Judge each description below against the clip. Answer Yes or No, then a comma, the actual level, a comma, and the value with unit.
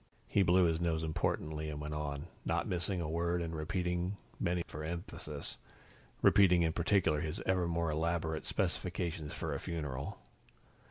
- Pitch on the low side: Yes, very low, 85 Hz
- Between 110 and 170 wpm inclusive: Yes, average, 155 wpm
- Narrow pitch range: Yes, narrow, 2.2 semitones